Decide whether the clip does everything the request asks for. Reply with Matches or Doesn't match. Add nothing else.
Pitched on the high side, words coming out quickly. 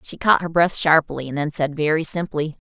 Doesn't match